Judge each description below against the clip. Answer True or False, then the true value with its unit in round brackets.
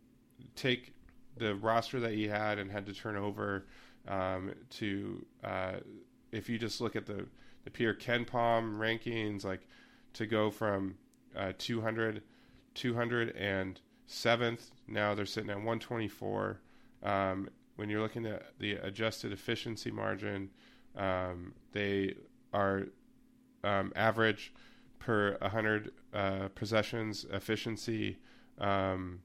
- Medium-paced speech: False (130 wpm)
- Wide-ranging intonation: False (2.7 semitones)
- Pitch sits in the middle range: False (105 Hz)